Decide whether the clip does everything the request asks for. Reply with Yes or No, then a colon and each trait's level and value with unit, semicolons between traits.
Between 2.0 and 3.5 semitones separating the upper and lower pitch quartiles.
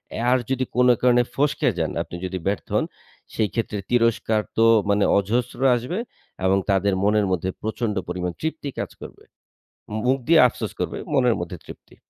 No: average, 4.2 semitones